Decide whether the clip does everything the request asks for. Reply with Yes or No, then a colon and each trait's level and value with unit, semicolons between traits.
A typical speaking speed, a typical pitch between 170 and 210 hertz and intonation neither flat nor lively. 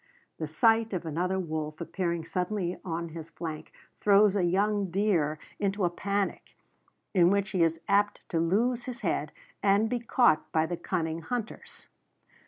Yes: average, 160 wpm; medium, 185 Hz; average, 3.8 semitones